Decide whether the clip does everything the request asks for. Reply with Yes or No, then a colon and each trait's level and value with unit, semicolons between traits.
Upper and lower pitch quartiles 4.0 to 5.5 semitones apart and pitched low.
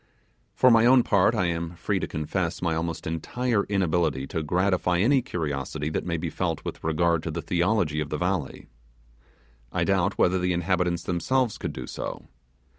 No: average, 3.2 semitones; very low, 85 Hz